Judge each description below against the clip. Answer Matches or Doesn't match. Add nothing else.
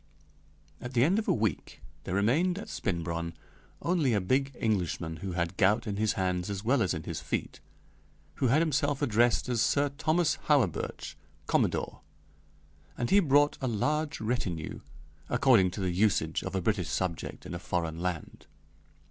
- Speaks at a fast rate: Doesn't match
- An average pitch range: Doesn't match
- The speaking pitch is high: Doesn't match